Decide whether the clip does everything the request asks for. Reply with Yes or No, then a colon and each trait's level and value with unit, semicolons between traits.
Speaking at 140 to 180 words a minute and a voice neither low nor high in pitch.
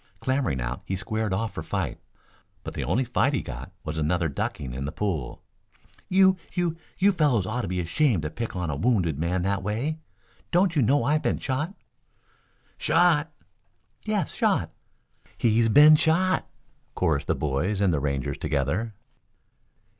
No: average, 160 wpm; low, 105 Hz